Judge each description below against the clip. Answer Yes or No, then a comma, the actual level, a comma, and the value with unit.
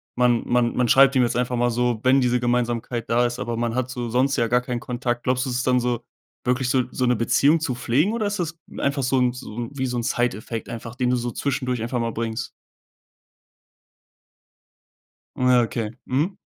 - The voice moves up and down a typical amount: No, narrow, 1.3 semitones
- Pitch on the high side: No, low, 125 Hz